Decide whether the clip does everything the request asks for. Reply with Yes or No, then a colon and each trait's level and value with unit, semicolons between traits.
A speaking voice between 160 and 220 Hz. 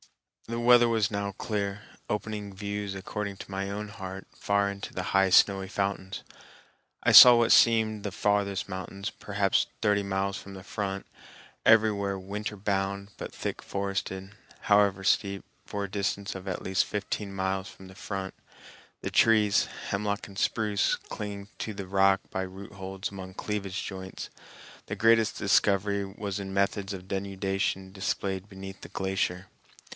No: low, 100 Hz